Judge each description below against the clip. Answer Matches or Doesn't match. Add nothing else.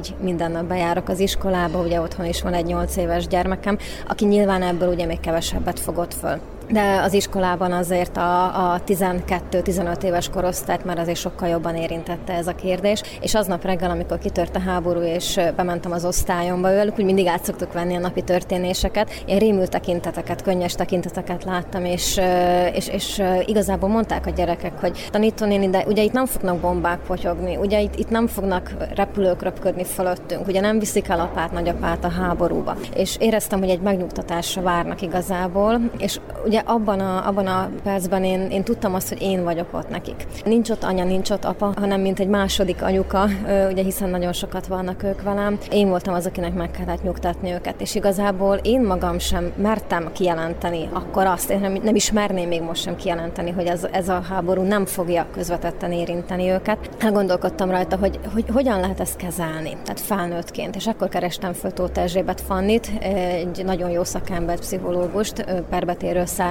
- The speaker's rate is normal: Doesn't match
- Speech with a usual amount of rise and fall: Doesn't match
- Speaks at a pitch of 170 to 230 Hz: Matches